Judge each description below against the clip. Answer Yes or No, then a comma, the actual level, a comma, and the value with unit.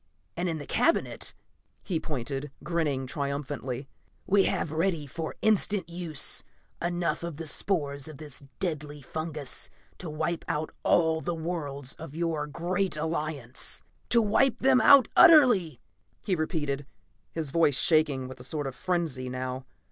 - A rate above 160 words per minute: No, average, 145 wpm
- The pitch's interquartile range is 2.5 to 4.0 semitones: Yes, average, 3.5 semitones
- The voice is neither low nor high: Yes, medium, 155 Hz